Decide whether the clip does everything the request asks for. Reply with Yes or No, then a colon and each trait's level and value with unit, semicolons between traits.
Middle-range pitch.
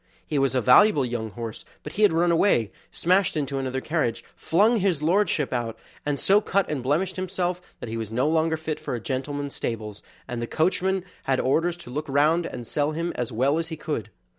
Yes: medium, 150 Hz